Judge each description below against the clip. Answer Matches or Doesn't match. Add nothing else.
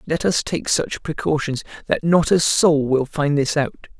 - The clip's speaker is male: Matches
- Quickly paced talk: Doesn't match